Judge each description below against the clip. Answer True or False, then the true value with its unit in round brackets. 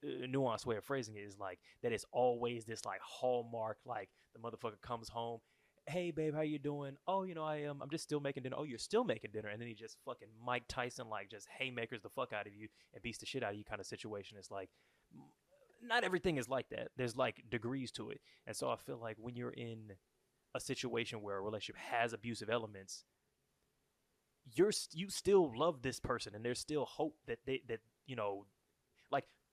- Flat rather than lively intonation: False (3.8 semitones)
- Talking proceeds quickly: True (225 wpm)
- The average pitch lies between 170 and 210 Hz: False (120 Hz)